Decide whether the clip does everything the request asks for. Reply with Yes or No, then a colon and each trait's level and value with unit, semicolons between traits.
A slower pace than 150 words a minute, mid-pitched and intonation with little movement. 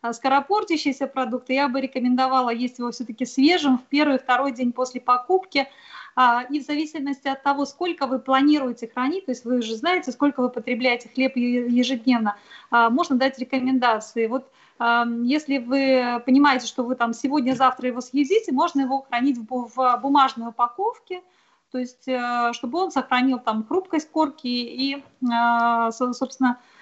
No: average, 140 wpm; very high, 260 Hz; narrow, 2.3 semitones